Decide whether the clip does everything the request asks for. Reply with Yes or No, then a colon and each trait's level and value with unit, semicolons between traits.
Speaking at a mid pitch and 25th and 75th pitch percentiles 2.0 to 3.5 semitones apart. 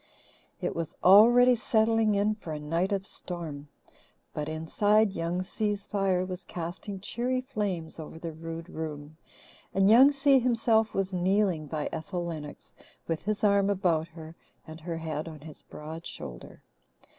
No: medium, 180 Hz; average, 4.7 semitones